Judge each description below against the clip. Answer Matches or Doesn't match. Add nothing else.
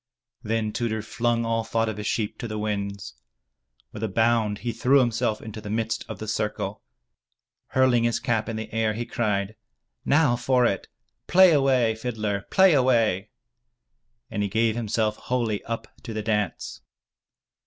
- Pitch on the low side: Matches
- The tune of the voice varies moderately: Doesn't match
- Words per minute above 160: Matches